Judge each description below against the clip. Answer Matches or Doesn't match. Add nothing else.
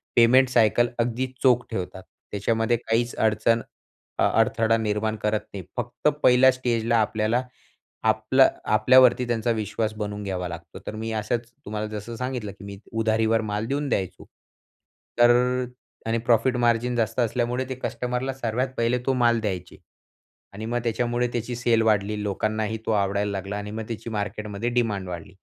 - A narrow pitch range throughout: Matches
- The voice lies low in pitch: Matches